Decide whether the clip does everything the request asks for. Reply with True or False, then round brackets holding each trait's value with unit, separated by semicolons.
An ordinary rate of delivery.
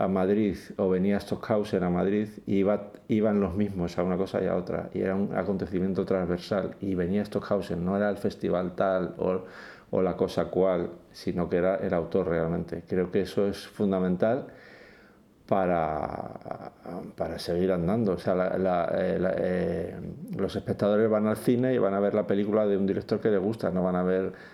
False (195 wpm)